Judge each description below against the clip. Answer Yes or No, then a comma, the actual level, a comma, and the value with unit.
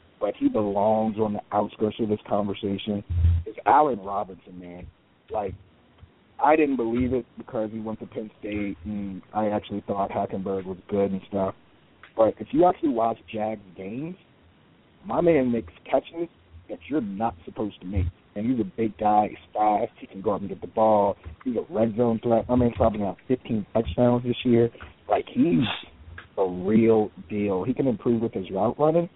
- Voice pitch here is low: Yes, low, 105 Hz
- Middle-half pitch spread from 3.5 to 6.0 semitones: No, average, 2.9 semitones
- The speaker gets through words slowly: No, average, 185 wpm